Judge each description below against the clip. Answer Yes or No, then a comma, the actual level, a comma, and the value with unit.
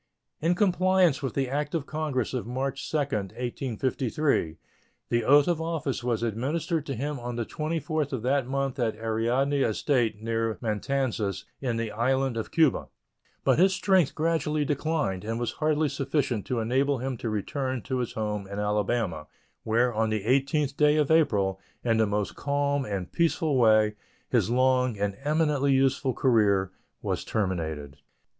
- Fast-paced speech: No, average, 160 wpm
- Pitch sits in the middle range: No, low, 130 Hz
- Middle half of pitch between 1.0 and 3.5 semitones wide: No, average, 4.7 semitones